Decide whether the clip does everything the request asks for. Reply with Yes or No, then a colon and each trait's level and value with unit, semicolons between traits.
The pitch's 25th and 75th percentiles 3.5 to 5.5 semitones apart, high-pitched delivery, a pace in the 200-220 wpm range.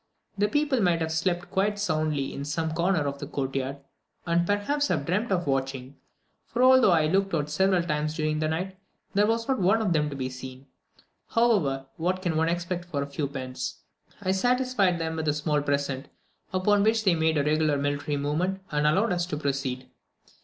No: average, 5.0 semitones; medium, 160 Hz; fast, 205 wpm